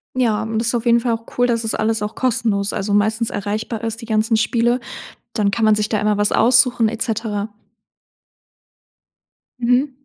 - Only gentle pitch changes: Yes, narrow, 1.8 semitones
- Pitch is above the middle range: Yes, high, 225 Hz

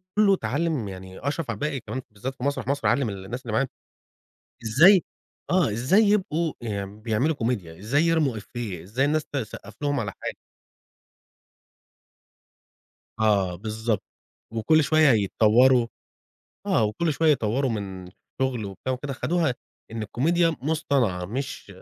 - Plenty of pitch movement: Yes, wide, 5.9 semitones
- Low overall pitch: Yes, low, 125 Hz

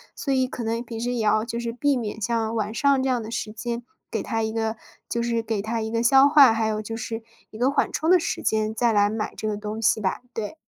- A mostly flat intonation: Yes, narrow, 1.8 semitones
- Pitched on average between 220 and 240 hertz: Yes, high, 225 Hz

